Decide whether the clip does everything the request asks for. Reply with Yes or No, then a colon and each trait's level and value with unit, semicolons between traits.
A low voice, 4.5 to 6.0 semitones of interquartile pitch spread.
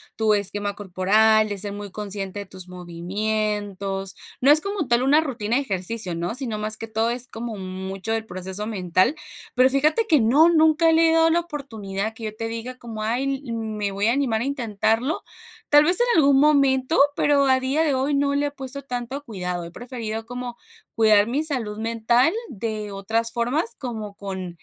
No: high, 225 Hz; average, 5.0 semitones